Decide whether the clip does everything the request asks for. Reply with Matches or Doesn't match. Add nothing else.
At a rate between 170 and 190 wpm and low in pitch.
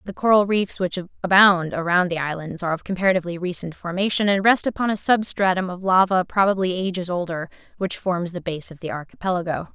Doesn't match